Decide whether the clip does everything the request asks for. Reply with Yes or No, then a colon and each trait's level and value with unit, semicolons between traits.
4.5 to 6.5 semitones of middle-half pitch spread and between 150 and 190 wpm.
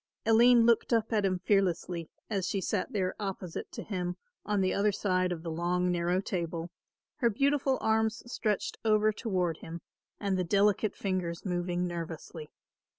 No: average, 3.4 semitones; average, 160 wpm